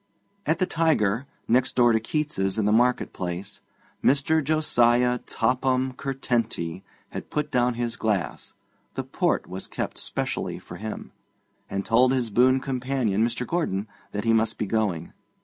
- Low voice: Yes, low, 120 Hz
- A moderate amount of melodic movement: Yes, average, 3.8 semitones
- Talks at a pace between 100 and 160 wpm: Yes, average, 150 wpm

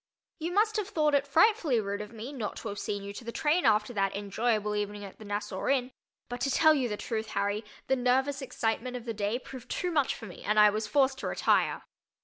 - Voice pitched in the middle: No, high, 235 Hz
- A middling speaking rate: No, fast, 240 wpm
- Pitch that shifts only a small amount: No, average, 4.8 semitones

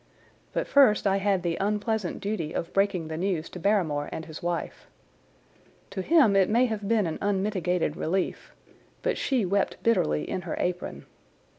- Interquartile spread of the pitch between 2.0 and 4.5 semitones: Yes, average, 3.5 semitones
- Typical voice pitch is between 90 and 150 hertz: No, high, 195 Hz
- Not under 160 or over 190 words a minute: Yes, average, 165 wpm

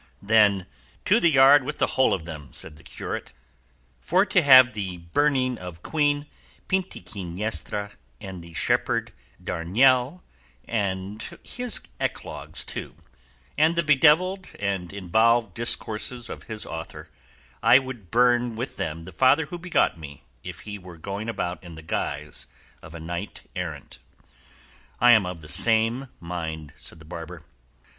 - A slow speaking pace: No, average, 145 wpm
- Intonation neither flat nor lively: No, wide, 7.2 semitones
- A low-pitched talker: Yes, low, 105 Hz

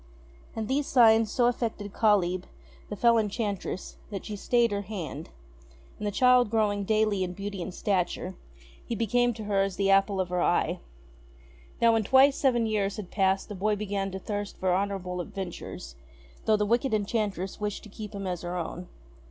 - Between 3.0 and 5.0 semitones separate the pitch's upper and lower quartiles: No, narrow, 2.5 semitones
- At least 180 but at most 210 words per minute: Yes, average, 185 wpm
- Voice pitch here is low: No, high, 205 Hz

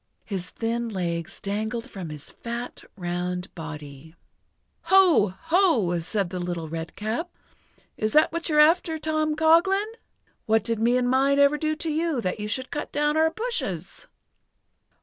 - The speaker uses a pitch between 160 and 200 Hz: No, high, 235 Hz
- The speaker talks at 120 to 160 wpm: Yes, average, 150 wpm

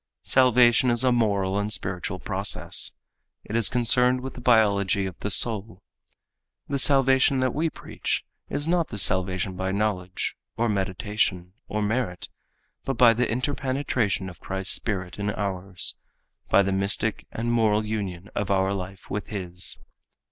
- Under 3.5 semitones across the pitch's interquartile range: No, average, 4.2 semitones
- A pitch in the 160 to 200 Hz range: No, low, 105 Hz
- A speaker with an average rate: Yes, average, 150 wpm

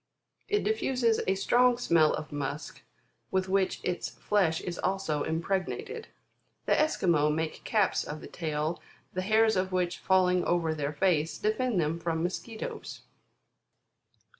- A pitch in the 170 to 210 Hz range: Yes, medium, 185 Hz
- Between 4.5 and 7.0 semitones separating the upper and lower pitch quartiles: Yes, average, 5.0 semitones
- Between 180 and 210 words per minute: No, average, 140 wpm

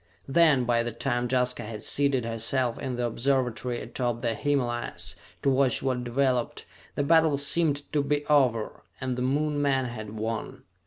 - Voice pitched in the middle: No, low, 125 Hz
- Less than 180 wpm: Yes, average, 165 wpm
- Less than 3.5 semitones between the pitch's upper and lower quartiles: Yes, average, 2.9 semitones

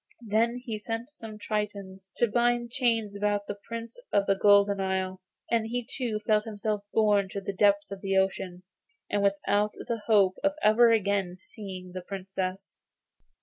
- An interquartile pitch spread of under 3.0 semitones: Yes, narrow, 2.6 semitones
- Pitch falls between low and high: No, high, 205 Hz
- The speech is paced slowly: No, average, 165 wpm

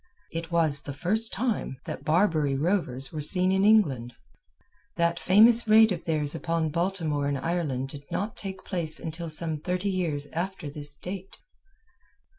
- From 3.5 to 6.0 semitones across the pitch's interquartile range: Yes, average, 4.4 semitones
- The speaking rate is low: No, average, 155 wpm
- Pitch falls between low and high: Yes, medium, 170 Hz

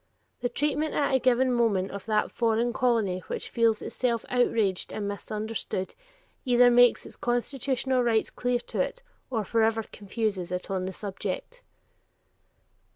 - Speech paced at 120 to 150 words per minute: Yes, average, 145 wpm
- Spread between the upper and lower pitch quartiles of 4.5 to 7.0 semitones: No, average, 3.0 semitones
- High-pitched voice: Yes, high, 230 Hz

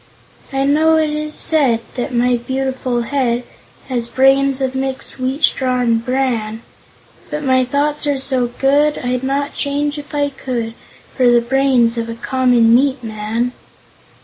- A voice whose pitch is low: No, very high, 260 Hz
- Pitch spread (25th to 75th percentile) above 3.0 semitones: No, narrow, 2.6 semitones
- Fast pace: No, average, 155 wpm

